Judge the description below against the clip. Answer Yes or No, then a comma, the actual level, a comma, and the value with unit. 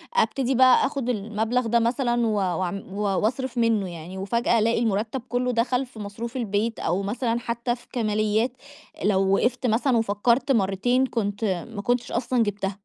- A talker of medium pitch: No, high, 230 Hz